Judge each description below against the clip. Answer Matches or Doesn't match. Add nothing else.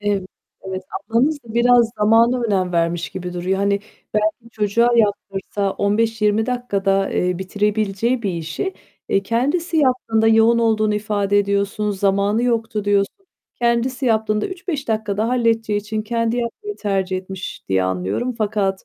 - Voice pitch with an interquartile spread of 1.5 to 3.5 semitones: Matches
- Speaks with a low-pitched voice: Doesn't match